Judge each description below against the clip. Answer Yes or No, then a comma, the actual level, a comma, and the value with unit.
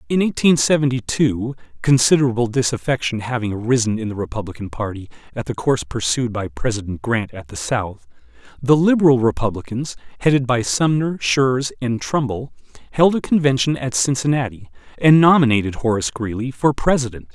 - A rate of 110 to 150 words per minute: Yes, average, 145 wpm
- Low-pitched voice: Yes, low, 125 Hz